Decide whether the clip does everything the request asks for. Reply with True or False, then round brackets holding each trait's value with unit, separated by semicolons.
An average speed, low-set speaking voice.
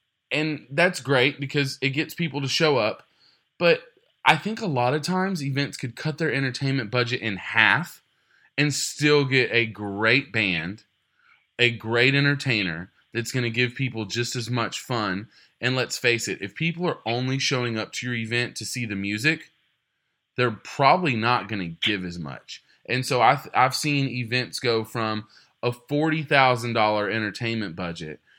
True (170 wpm; 125 Hz)